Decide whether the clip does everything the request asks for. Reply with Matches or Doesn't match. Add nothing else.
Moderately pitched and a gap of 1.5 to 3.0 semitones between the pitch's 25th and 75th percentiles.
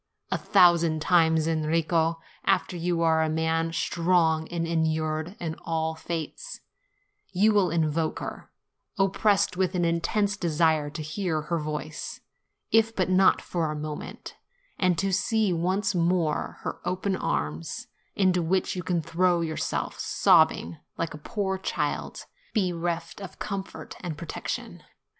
Matches